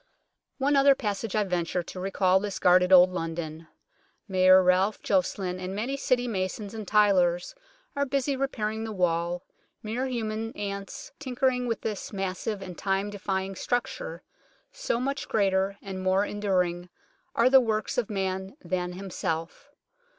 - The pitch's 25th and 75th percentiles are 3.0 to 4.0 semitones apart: Yes, average, 3.6 semitones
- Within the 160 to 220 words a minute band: No, average, 145 wpm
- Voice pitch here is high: Yes, high, 195 Hz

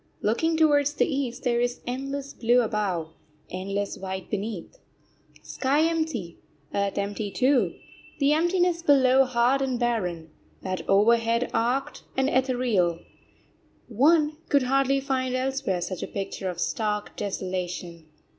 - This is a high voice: Yes, high, 245 Hz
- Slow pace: Yes, slow, 125 wpm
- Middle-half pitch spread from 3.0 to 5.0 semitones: No, wide, 5.6 semitones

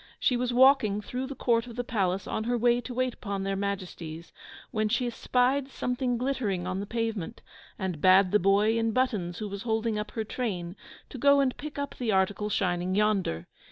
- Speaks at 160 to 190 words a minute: No, average, 200 wpm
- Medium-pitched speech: No, high, 215 Hz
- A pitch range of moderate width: Yes, average, 4.2 semitones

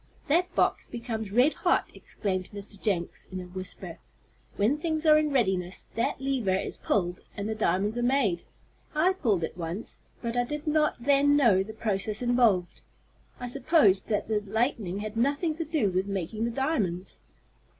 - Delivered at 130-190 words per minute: Yes, average, 170 wpm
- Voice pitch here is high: Yes, high, 220 Hz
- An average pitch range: No, wide, 6.2 semitones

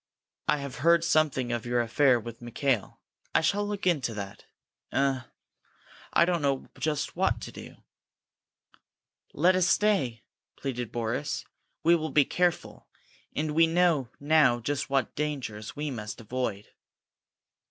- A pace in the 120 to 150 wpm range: Yes, average, 140 wpm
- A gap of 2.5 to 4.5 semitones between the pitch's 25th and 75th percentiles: No, average, 5.2 semitones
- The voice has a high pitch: No, medium, 140 Hz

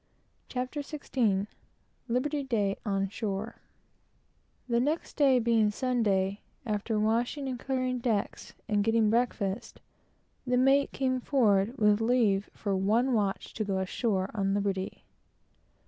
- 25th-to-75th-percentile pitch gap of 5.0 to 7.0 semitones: No, average, 4.0 semitones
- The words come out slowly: Yes, slow, 125 wpm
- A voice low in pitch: No, high, 225 Hz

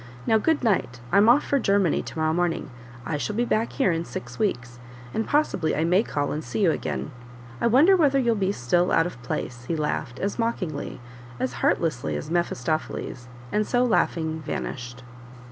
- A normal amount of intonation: No, wide, 8.4 semitones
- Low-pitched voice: No, medium, 170 Hz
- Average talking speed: Yes, average, 185 wpm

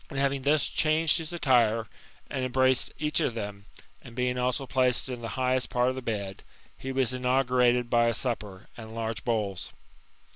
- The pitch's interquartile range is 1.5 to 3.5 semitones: Yes, narrow, 2.4 semitones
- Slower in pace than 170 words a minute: No, average, 180 wpm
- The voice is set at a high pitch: No, low, 125 Hz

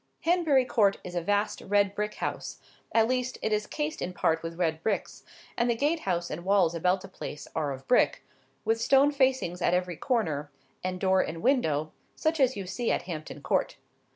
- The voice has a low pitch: No, high, 200 Hz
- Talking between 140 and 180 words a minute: No, average, 190 wpm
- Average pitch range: No, wide, 6.5 semitones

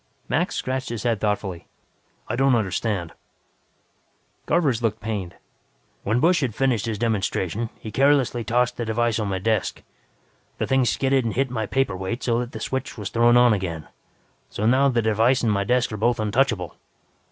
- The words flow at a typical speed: Yes, average, 175 wpm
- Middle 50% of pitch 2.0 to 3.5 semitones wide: Yes, average, 3.2 semitones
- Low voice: Yes, low, 115 Hz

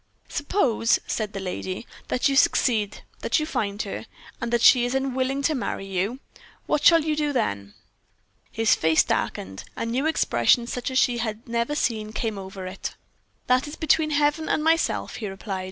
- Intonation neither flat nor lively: No, wide, 5.9 semitones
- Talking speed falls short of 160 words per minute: No, average, 180 wpm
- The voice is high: Yes, high, 235 Hz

